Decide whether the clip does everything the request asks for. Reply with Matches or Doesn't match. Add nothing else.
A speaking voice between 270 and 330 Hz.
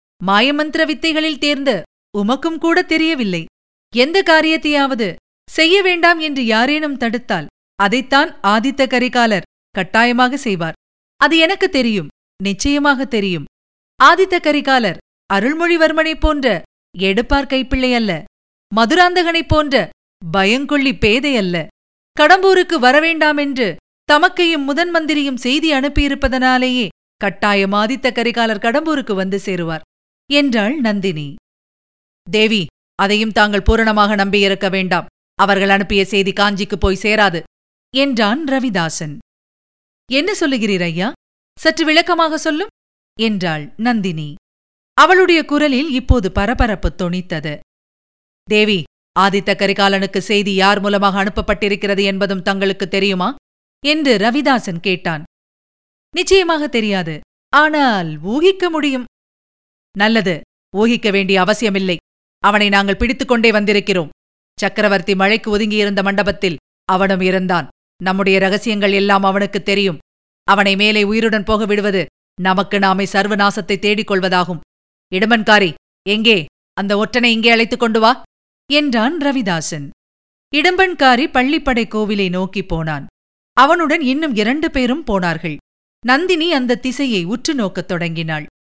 Doesn't match